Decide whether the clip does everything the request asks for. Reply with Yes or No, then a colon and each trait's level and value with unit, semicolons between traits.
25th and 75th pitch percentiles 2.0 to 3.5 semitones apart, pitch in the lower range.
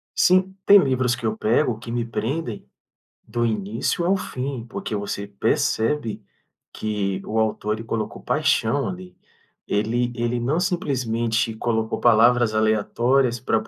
Yes: average, 3.0 semitones; low, 115 Hz